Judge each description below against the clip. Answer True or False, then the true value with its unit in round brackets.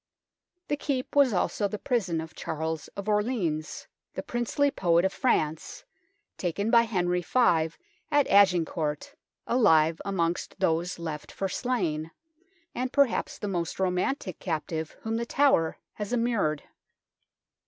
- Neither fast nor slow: False (130 wpm)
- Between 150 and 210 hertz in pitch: True (190 Hz)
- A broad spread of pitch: True (6.5 semitones)